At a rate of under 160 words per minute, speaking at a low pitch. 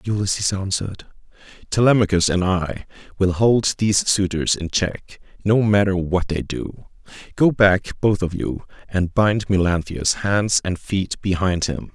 Yes: average, 145 wpm; very low, 95 Hz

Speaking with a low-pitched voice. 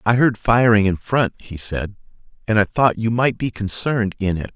Yes: low, 110 Hz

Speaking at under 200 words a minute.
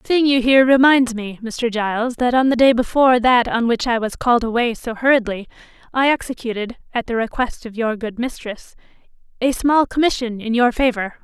Yes: average, 190 wpm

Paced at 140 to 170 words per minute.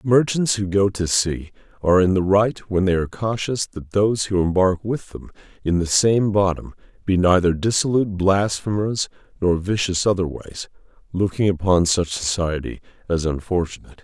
Yes: average, 160 wpm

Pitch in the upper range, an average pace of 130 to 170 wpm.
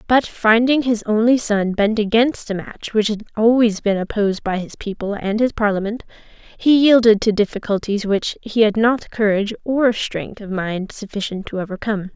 No: high, 215 Hz; average, 180 wpm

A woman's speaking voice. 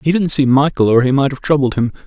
No: male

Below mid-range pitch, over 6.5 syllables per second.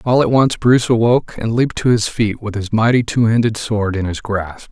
No: low, 110 Hz; 5.5 syllables/s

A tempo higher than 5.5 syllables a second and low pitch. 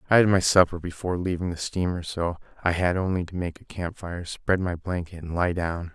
Yes: 5.7 syllables/s; very low, 90 Hz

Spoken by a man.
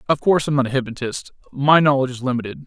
Yes: male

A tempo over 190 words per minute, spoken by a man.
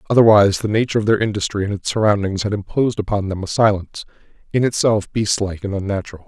Yes: average, 200 wpm; male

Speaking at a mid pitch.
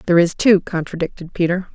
Yes: medium, 175 Hz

